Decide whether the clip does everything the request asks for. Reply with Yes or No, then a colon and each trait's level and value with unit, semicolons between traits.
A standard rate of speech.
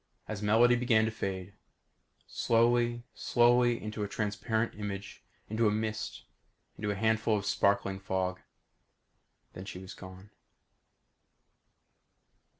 No: slow, 115 wpm